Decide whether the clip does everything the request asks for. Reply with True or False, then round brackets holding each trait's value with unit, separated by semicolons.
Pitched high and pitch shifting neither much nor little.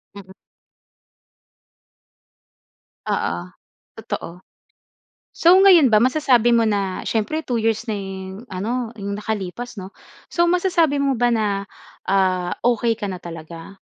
True (220 Hz; 4.6 semitones)